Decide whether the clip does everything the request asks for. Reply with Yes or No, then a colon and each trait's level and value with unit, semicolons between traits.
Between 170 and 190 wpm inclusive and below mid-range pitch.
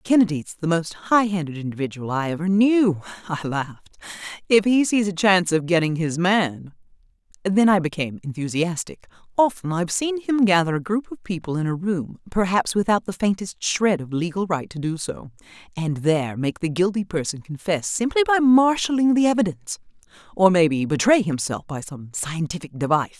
No: average, 175 wpm; medium, 180 Hz